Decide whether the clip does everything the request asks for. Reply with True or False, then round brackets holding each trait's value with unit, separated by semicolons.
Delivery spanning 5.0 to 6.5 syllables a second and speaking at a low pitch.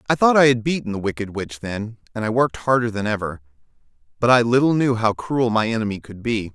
True (6.1 syllables/s; 115 Hz)